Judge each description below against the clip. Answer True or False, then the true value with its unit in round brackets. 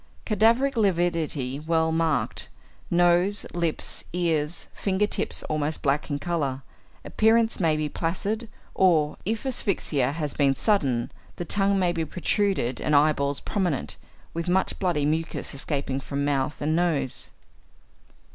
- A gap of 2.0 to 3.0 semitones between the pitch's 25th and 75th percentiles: False (4.6 semitones)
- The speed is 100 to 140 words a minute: True (135 wpm)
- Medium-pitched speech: True (165 Hz)